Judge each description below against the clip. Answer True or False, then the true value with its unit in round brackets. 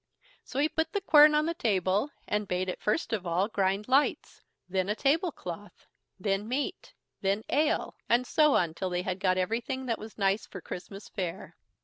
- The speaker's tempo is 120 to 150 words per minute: False (195 wpm)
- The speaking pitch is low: False (210 Hz)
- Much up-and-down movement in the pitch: True (6.4 semitones)